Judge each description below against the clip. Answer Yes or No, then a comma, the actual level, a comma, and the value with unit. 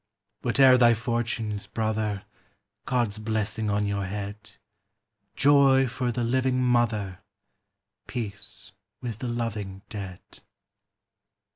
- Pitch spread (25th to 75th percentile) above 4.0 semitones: No, average, 3.0 semitones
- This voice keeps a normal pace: No, slow, 100 wpm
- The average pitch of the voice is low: Yes, low, 110 Hz